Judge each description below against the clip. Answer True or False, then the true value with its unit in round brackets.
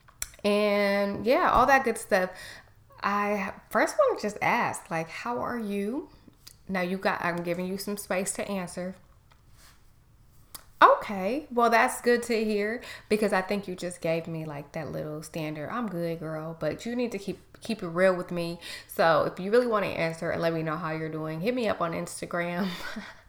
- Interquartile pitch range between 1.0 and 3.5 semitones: False (4.3 semitones)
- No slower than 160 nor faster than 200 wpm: True (195 wpm)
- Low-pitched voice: False (190 Hz)